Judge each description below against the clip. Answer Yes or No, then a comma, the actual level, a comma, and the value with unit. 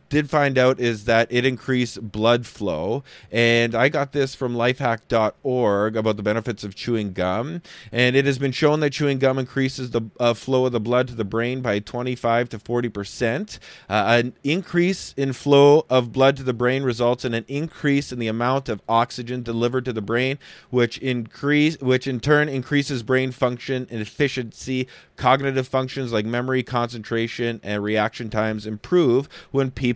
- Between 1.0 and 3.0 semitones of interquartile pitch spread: Yes, narrow, 2.5 semitones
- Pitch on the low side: Yes, low, 125 Hz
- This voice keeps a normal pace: Yes, average, 175 wpm